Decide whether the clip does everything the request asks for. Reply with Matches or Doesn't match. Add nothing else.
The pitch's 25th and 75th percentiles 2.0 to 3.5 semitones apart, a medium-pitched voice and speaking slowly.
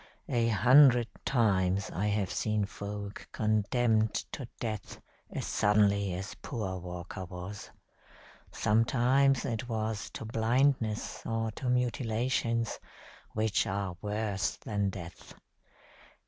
Doesn't match